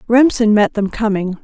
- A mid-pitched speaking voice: No, high, 215 Hz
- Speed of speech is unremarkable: Yes, average, 165 wpm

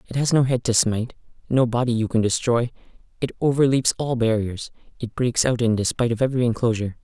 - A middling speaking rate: Yes, average, 195 wpm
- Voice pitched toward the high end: No, low, 120 Hz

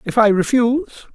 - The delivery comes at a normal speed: Yes, average, 155 wpm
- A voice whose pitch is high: Yes, high, 240 Hz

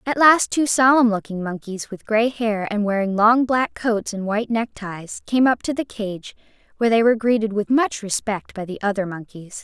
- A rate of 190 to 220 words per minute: Yes, fast, 205 wpm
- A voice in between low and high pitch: No, high, 220 Hz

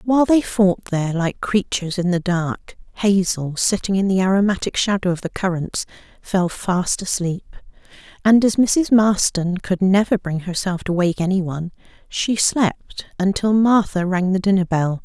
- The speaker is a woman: Yes, female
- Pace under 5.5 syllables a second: Yes, 4.6 syllables/s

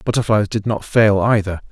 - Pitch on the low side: Yes, low, 105 Hz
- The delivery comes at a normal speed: Yes, average, 175 wpm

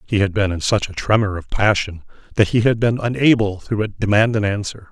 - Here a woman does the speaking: No, male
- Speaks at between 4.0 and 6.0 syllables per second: Yes, 5.5 syllables/s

